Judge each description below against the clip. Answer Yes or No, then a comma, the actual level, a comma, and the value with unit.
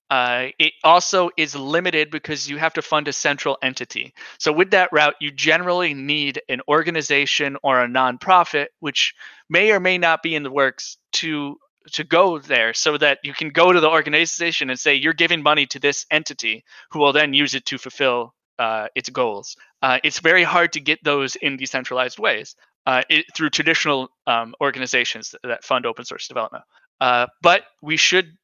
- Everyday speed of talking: Yes, average, 190 wpm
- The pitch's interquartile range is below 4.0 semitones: Yes, average, 2.9 semitones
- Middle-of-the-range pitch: Yes, medium, 150 Hz